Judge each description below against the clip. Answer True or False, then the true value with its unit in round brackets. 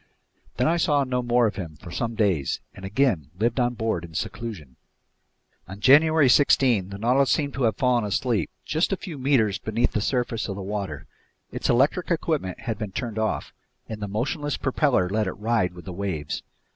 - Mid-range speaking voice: False (115 Hz)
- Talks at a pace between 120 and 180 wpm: False (195 wpm)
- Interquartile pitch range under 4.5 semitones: False (5.2 semitones)